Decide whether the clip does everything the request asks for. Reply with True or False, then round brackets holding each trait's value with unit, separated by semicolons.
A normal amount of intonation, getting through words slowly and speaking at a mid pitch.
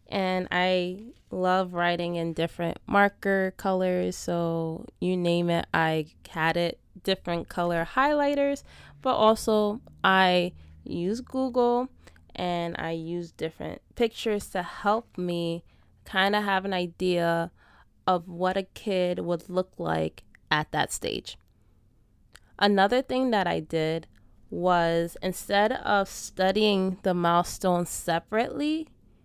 True (3.2 semitones; 120 wpm; 180 Hz)